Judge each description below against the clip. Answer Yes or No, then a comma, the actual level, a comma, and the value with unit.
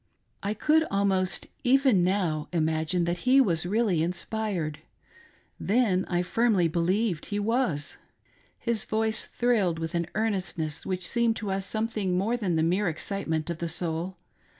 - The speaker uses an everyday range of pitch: Yes, average, 4.4 semitones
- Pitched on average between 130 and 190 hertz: Yes, medium, 185 Hz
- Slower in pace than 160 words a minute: Yes, average, 150 wpm